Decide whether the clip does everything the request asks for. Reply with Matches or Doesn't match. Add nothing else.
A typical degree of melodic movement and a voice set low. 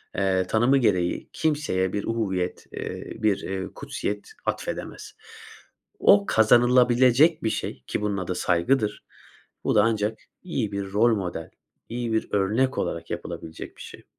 Matches